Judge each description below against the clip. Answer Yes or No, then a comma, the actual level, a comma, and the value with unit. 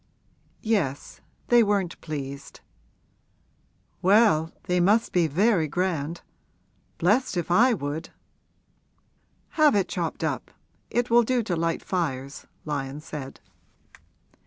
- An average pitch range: No, wide, 6.1 semitones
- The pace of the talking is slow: Yes, slow, 110 wpm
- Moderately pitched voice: Yes, medium, 175 Hz